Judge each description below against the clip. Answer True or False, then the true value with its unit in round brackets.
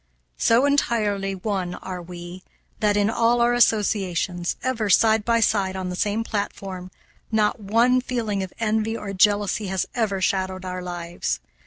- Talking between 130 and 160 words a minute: True (155 wpm)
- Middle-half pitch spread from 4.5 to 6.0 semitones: False (3.1 semitones)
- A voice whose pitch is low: False (205 Hz)